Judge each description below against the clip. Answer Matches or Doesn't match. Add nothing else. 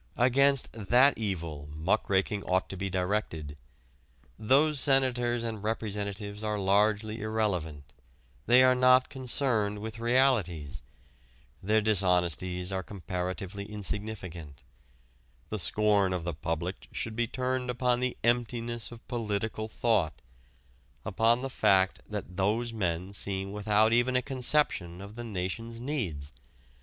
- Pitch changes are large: Doesn't match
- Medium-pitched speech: Doesn't match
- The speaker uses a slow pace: Matches